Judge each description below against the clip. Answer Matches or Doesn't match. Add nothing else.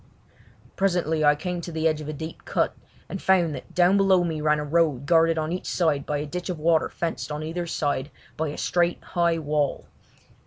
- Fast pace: Matches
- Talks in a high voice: Doesn't match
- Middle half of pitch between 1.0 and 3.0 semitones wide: Matches